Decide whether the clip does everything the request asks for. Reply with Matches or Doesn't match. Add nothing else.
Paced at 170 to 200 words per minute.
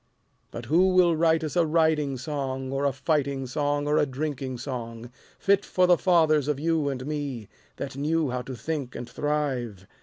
Matches